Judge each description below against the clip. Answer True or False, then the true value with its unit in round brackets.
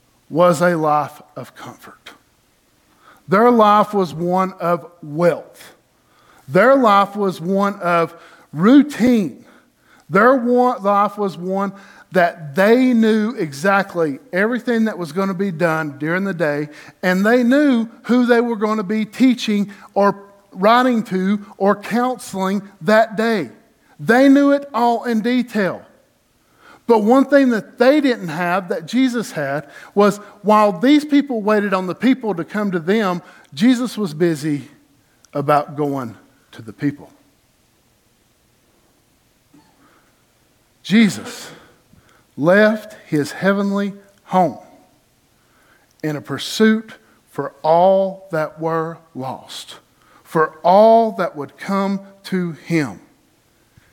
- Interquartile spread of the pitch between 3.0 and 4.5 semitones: False (5.0 semitones)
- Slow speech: True (120 wpm)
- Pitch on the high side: True (195 Hz)